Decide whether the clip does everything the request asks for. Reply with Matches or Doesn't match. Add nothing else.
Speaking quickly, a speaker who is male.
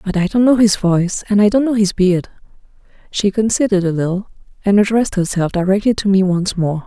Doesn't match